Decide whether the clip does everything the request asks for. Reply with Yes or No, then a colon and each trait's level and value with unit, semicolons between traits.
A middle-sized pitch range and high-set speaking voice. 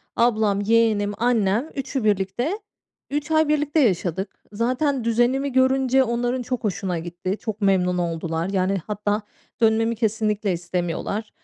Yes: average, 4.5 semitones; high, 220 Hz